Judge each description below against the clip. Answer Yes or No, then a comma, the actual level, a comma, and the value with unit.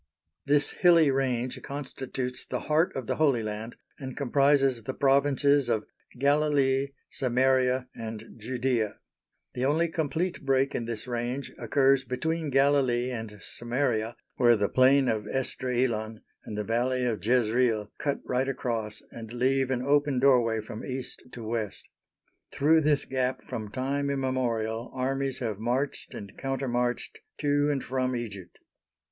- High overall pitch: No, low, 130 Hz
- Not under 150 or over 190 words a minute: No, average, 140 wpm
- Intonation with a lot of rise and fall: No, average, 2.7 semitones